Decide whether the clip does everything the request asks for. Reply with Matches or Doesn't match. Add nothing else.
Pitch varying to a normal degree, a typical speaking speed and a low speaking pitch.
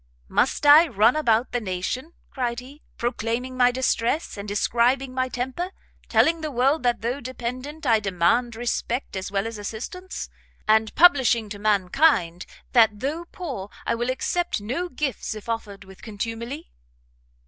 Doesn't match